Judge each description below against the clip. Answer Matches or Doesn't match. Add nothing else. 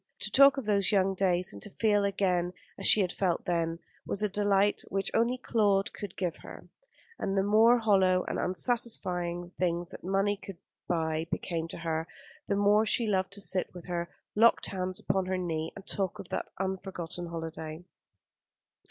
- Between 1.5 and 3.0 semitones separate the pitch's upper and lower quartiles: Matches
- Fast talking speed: Doesn't match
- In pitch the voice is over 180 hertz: Matches